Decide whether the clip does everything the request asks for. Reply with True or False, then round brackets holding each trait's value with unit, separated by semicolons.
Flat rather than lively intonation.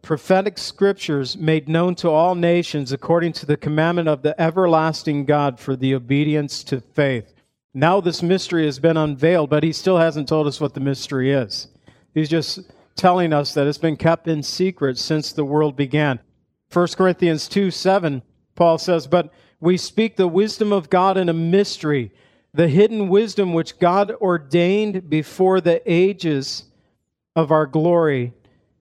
False (3.4 semitones)